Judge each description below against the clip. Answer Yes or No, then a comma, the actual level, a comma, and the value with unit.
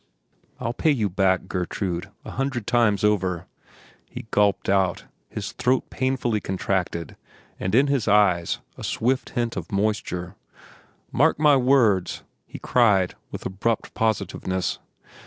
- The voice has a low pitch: Yes, low, 105 Hz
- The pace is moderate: No, slow, 130 wpm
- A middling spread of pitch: Yes, average, 4.5 semitones